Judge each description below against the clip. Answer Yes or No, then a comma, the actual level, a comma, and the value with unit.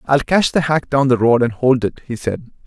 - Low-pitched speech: Yes, low, 130 Hz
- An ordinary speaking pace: No, fast, 270 wpm